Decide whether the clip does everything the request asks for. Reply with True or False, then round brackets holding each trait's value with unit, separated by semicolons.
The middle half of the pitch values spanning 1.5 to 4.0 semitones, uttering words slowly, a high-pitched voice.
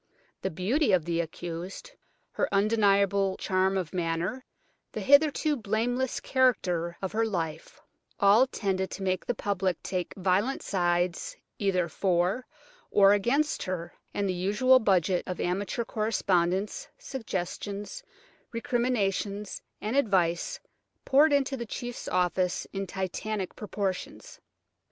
False (4.4 semitones; 120 wpm; 195 Hz)